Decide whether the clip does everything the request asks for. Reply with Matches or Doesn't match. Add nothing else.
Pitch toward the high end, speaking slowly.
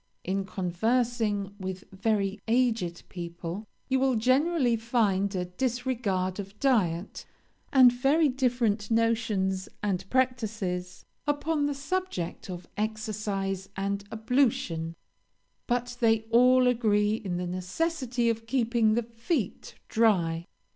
Matches